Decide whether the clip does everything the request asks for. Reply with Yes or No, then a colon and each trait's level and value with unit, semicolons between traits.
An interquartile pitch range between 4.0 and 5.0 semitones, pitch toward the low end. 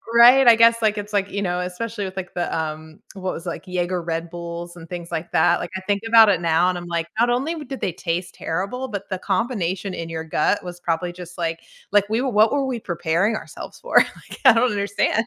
No: average, 4.3 semitones; medium, 185 Hz